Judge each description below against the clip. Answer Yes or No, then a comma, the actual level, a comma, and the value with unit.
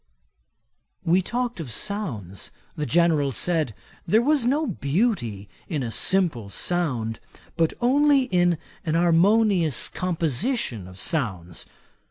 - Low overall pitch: No, medium, 170 Hz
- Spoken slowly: Yes, slow, 115 wpm